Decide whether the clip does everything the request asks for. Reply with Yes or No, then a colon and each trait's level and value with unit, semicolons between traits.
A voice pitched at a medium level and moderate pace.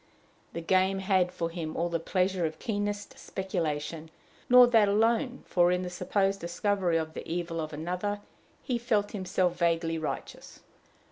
Yes: medium, 180 Hz; average, 155 wpm